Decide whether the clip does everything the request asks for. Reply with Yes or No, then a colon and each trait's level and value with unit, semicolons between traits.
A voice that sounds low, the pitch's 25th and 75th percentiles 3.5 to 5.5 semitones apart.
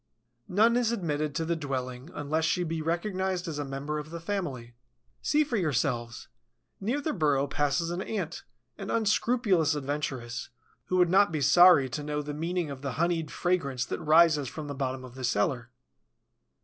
No: medium, 155 Hz; average, 4.6 semitones